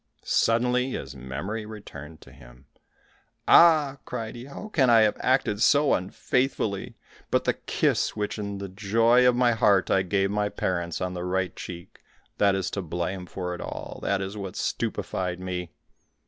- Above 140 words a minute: Yes, average, 170 wpm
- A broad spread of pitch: No, average, 4.4 semitones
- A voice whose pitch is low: Yes, low, 100 Hz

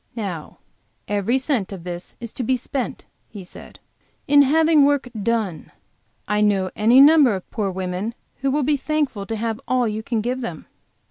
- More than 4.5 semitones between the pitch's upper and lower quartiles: Yes, average, 5.1 semitones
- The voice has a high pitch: Yes, high, 230 Hz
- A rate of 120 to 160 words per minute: No, average, 180 wpm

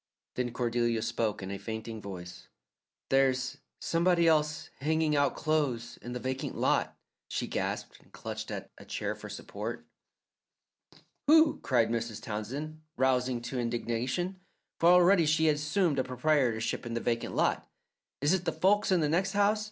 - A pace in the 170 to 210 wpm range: No, average, 160 wpm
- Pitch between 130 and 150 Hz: Yes, low, 135 Hz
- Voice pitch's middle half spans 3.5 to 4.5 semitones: No, wide, 5.4 semitones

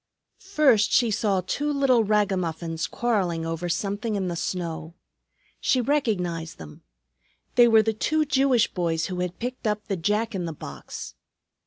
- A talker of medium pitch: No, high, 205 Hz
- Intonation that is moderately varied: No, wide, 5.8 semitones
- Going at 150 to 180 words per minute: Yes, average, 155 wpm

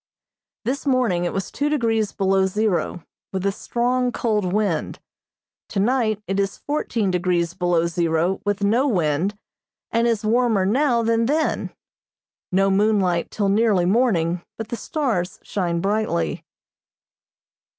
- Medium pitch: No, high, 205 Hz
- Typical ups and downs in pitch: Yes, average, 4.3 semitones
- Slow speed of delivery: Yes, slow, 130 wpm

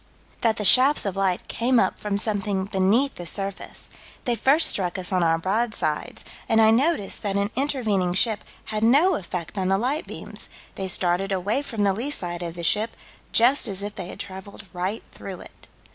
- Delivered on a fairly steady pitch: No, average, 3.6 semitones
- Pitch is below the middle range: No, high, 200 Hz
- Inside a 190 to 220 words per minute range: Yes, average, 195 wpm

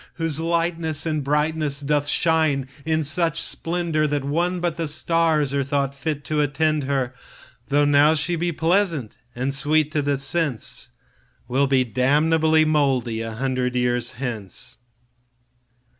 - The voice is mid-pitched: Yes, medium, 150 Hz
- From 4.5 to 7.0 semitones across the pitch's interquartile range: No, average, 3.0 semitones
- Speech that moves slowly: Yes, slow, 130 wpm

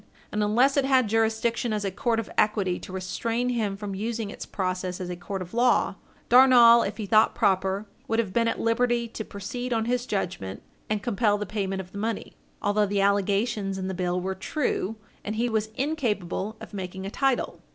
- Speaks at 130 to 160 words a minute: No, fast, 205 wpm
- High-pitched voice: Yes, high, 210 Hz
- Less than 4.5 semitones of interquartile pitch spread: Yes, average, 3.3 semitones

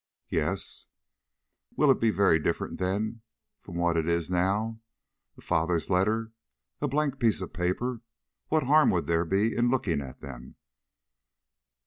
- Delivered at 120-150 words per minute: Yes, average, 145 wpm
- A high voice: No, very low, 95 Hz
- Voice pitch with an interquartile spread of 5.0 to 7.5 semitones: Yes, wide, 5.4 semitones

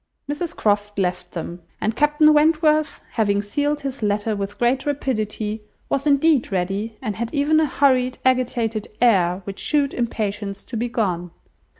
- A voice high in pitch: Yes, high, 230 Hz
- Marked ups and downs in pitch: Yes, wide, 5.7 semitones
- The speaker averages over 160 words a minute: No, average, 155 wpm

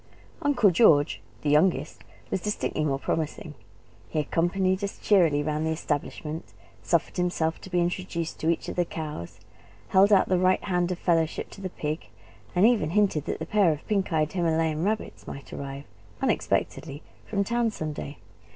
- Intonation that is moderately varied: Yes, average, 3.8 semitones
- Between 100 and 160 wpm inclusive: No, average, 170 wpm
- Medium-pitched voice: Yes, medium, 170 Hz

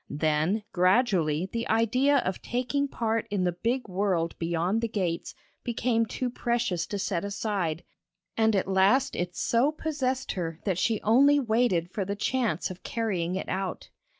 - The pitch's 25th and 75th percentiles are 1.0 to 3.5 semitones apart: No, average, 5.0 semitones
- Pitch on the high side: Yes, high, 205 Hz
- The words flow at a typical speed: Yes, average, 160 wpm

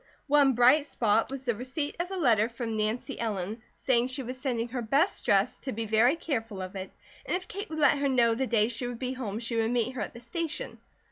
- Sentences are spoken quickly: Yes, fast, 245 wpm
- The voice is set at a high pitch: Yes, high, 245 Hz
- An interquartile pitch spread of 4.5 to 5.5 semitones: No, average, 3.3 semitones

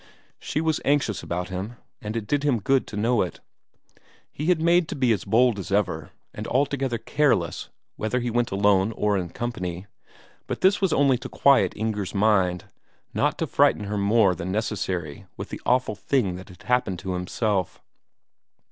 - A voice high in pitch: No, low, 110 Hz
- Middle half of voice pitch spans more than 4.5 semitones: Yes, average, 5.2 semitones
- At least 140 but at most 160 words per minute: No, average, 180 wpm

